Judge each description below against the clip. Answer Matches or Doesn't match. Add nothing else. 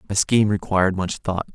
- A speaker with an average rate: Matches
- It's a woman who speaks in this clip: Doesn't match